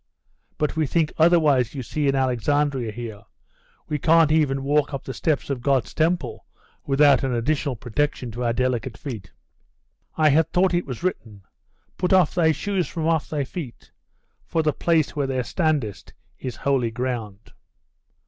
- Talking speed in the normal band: Yes, average, 165 wpm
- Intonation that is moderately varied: Yes, average, 4.1 semitones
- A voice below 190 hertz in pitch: Yes, medium, 140 Hz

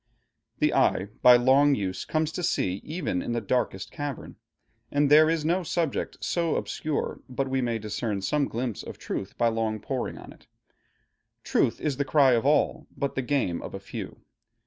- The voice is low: Yes, low, 130 Hz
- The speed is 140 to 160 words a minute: No, average, 185 wpm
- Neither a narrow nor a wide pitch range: Yes, average, 4.7 semitones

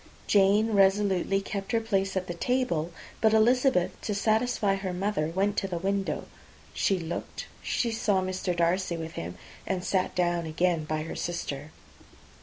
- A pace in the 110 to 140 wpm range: No, average, 160 wpm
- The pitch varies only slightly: No, average, 3.1 semitones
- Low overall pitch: No, high, 190 Hz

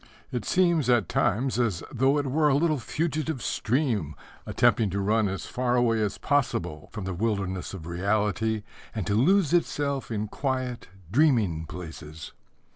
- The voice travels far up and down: Yes, wide, 5.7 semitones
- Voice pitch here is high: No, low, 115 Hz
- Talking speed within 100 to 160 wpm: Yes, average, 155 wpm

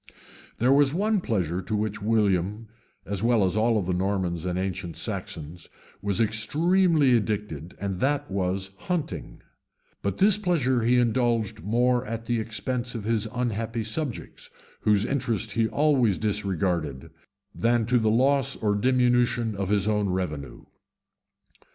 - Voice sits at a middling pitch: No, low, 110 Hz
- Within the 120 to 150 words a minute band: Yes, average, 145 wpm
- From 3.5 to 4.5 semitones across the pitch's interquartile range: Yes, average, 4.1 semitones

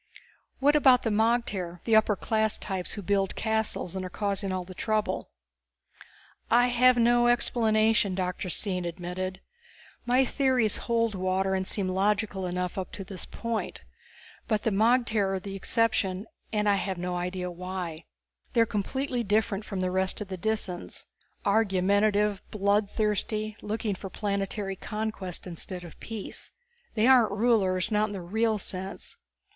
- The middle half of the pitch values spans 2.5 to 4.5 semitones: Yes, average, 2.8 semitones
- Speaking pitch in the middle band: No, high, 205 Hz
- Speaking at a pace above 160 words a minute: No, average, 155 wpm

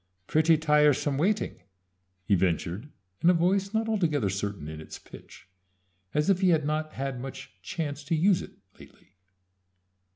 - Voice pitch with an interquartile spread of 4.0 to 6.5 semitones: Yes, average, 5.1 semitones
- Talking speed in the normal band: Yes, average, 155 wpm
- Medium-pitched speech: Yes, medium, 150 Hz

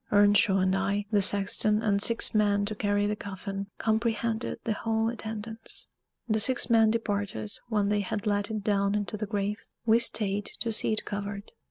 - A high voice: Yes, high, 210 Hz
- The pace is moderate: Yes, average, 180 wpm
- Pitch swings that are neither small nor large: No, narrow, 1.5 semitones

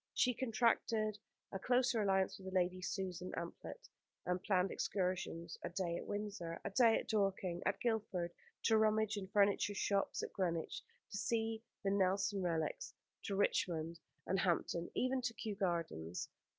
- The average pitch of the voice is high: Yes, high, 195 Hz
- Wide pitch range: No, average, 3.3 semitones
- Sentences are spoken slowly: No, average, 150 wpm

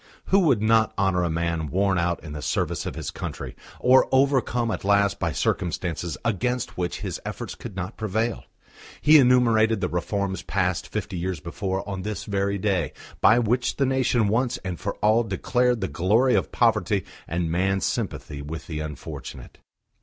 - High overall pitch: No, low, 100 Hz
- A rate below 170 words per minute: No, average, 175 wpm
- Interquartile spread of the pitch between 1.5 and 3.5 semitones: No, average, 4.8 semitones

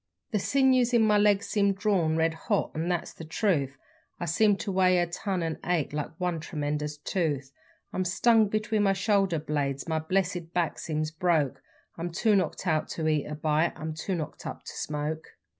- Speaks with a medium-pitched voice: Yes, medium, 170 Hz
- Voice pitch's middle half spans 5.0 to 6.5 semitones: No, average, 4.1 semitones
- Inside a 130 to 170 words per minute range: No, average, 190 wpm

